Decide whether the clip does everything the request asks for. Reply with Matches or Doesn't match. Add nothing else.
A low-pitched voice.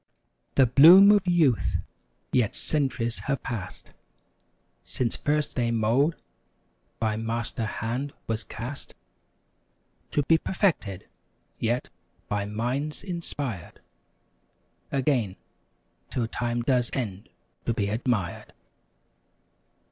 Matches